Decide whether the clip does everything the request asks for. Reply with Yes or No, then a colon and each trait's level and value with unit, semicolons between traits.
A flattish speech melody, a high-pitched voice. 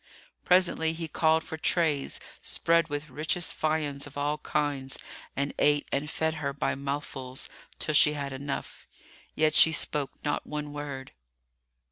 No: narrow, 2.0 semitones; medium, 150 Hz